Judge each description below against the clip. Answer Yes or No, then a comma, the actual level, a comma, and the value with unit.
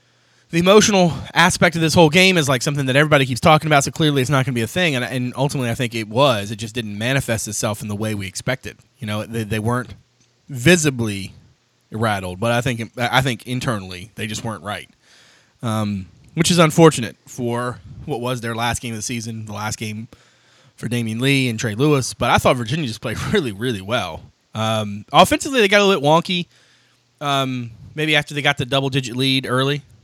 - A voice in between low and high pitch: No, low, 125 Hz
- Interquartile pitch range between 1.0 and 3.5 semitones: No, average, 4.2 semitones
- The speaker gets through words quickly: Yes, fast, 210 wpm